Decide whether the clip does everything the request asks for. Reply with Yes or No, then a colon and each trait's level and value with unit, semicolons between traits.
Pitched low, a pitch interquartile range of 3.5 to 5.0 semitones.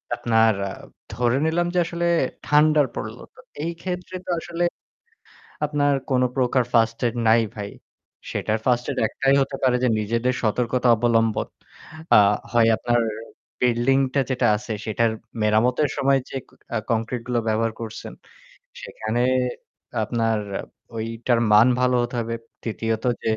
No: low, 120 Hz; average, 3.0 semitones